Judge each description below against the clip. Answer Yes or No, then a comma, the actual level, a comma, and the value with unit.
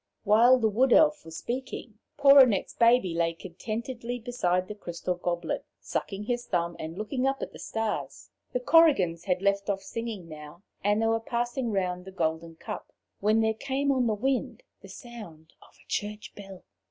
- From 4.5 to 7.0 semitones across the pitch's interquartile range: Yes, average, 5.2 semitones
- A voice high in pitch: Yes, high, 215 Hz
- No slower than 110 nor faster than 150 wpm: No, average, 180 wpm